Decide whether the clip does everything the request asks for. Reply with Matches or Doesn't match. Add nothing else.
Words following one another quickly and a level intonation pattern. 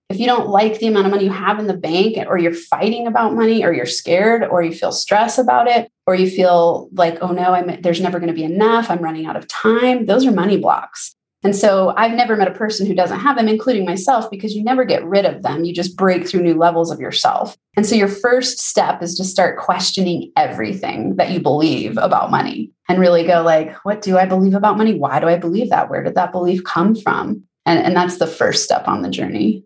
Doesn't match